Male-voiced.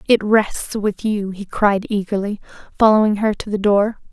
No: female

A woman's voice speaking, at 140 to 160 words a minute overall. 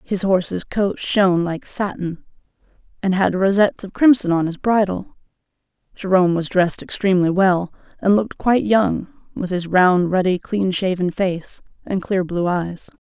Yes: female; average, 155 wpm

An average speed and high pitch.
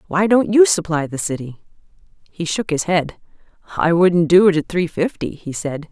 No: average, 195 wpm; medium, 170 Hz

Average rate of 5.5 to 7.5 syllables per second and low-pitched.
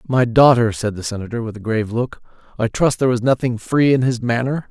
Yes: 6.0 syllables/s; low, 120 Hz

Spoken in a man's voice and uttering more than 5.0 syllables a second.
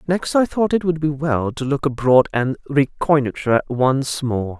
No: male; 4.3 syllables/s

